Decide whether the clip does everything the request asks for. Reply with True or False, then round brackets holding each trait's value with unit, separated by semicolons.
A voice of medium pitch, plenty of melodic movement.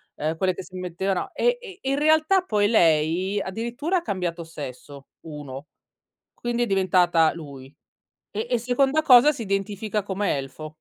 False (195 Hz; 6.9 semitones)